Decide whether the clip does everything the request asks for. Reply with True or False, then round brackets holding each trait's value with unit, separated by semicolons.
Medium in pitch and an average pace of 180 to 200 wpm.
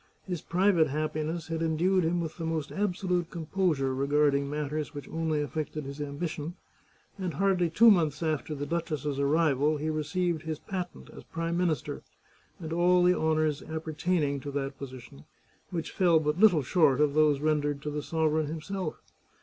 False (155 Hz; 165 wpm)